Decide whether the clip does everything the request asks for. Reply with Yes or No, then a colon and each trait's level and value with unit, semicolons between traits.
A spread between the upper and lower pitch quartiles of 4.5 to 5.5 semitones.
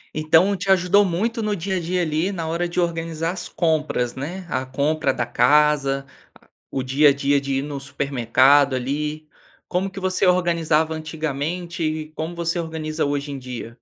No: average, 3.6 semitones